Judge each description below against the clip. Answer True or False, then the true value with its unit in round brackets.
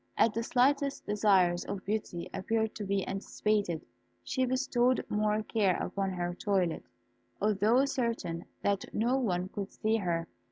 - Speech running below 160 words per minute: True (145 wpm)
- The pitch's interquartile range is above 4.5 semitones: False (3.6 semitones)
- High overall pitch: True (210 Hz)